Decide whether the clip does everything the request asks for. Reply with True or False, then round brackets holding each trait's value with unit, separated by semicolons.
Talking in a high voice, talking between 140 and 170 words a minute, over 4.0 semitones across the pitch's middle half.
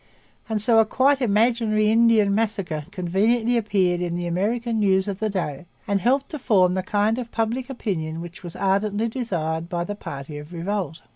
False (205 Hz; 185 wpm; 4.4 semitones)